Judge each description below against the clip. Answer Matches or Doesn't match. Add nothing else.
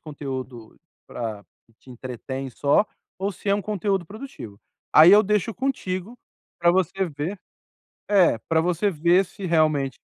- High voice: Doesn't match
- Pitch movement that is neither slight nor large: Doesn't match